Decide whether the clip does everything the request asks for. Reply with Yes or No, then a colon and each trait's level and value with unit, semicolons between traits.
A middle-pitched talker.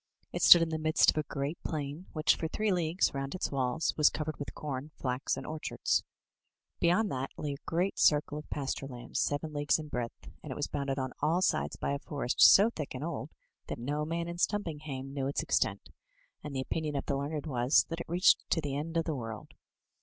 Yes: medium, 150 Hz